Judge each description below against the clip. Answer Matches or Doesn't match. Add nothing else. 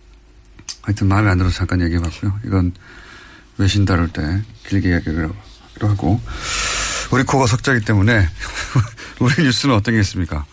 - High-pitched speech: Doesn't match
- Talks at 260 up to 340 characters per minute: Matches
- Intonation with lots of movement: Doesn't match